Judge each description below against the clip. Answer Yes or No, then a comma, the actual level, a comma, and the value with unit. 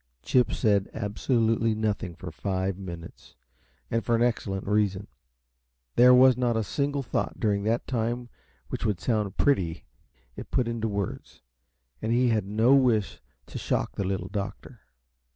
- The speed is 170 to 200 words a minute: No, average, 150 wpm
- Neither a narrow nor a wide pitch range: Yes, average, 3.4 semitones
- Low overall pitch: Yes, low, 110 Hz